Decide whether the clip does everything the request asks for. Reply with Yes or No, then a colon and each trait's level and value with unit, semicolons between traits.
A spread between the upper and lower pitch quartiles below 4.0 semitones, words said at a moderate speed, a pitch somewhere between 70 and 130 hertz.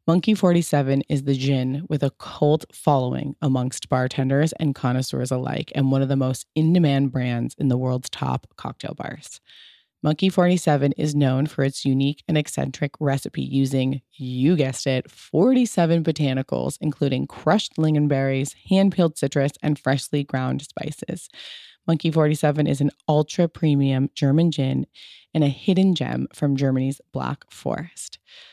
No: narrow, 2.6 semitones; average, 145 wpm; medium, 140 Hz